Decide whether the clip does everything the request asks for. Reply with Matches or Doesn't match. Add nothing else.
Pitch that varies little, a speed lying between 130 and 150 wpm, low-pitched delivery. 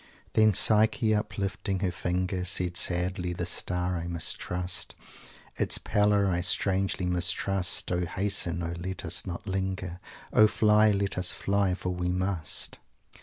Matches